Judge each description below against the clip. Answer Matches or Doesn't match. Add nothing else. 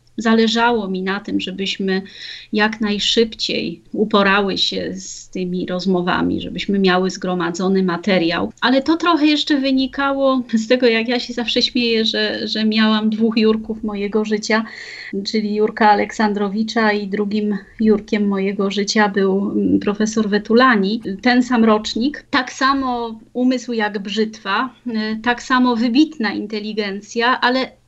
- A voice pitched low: Doesn't match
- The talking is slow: Doesn't match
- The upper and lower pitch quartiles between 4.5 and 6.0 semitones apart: Doesn't match